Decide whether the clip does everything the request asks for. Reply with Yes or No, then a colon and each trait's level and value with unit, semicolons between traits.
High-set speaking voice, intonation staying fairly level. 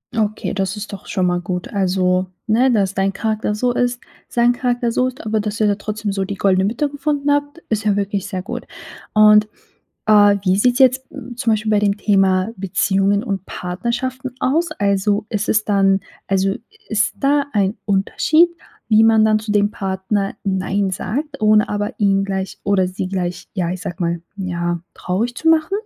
No: high, 205 Hz; average, 3.1 semitones